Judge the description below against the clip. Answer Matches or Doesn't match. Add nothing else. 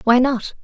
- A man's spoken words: Doesn't match